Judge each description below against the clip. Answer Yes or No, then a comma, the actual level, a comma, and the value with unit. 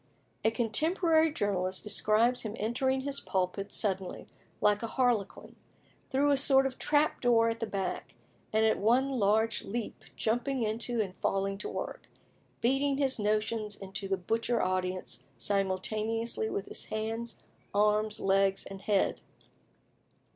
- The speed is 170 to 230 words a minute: No, average, 140 wpm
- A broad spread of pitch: No, average, 3.6 semitones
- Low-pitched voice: No, high, 220 Hz